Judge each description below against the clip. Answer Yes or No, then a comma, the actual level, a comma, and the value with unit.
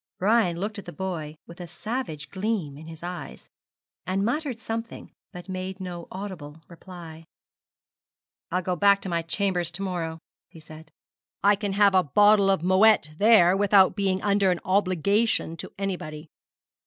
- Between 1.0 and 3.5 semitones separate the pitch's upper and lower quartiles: Yes, average, 3.1 semitones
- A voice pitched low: No, medium, 185 Hz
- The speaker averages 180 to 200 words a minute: No, average, 160 wpm